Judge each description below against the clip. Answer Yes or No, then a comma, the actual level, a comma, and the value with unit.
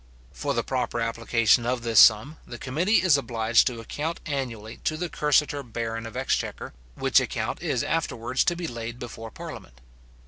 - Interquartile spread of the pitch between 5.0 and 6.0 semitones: No, average, 4.3 semitones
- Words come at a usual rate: Yes, average, 170 wpm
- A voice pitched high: No, low, 120 Hz